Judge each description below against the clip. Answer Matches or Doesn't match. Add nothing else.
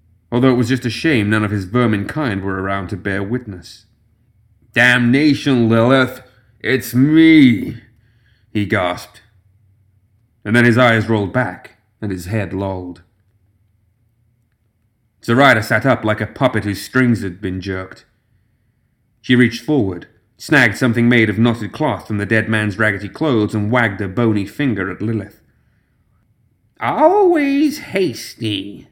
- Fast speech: Doesn't match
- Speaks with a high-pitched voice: Doesn't match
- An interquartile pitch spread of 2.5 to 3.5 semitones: Matches